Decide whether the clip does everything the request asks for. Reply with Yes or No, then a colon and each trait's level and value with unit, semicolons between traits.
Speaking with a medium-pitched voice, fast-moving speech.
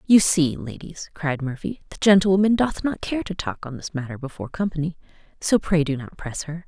Yes: medium, 165 Hz; fast, 215 wpm